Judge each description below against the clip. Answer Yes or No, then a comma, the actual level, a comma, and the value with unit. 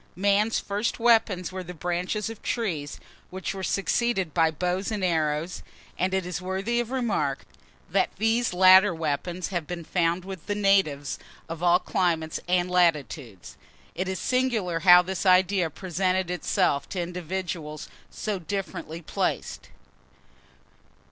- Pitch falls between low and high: Yes, medium, 180 Hz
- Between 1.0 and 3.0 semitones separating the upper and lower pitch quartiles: Yes, average, 2.7 semitones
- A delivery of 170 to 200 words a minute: No, average, 140 wpm